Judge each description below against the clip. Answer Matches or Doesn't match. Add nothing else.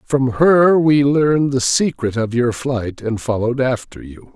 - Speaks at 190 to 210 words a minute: Doesn't match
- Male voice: Matches